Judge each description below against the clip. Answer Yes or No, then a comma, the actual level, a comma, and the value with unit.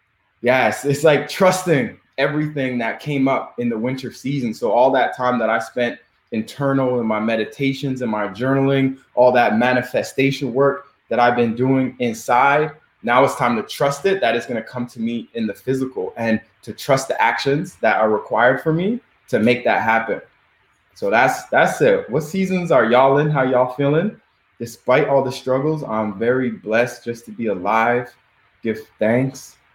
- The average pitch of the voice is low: Yes, low, 130 Hz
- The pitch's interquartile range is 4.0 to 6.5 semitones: No, average, 3.0 semitones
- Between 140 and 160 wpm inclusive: No, average, 180 wpm